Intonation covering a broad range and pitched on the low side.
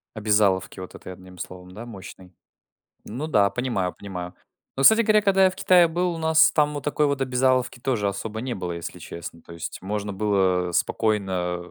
Yes: wide, 7.0 semitones; low, 105 Hz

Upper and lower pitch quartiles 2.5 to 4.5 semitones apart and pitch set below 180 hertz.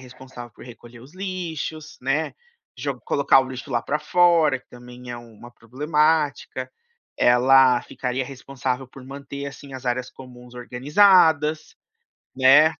Yes: average, 3.4 semitones; low, 135 Hz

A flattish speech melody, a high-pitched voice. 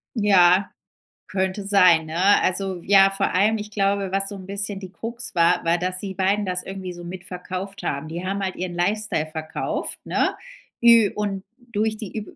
Yes: narrow, 2.2 semitones; high, 195 Hz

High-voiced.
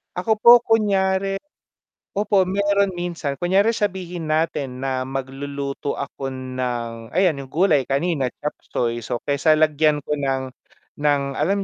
No: medium, 150 Hz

